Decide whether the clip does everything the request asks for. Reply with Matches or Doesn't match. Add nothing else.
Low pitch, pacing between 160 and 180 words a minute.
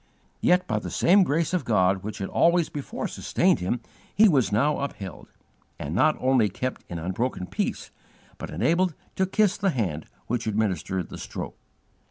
Matches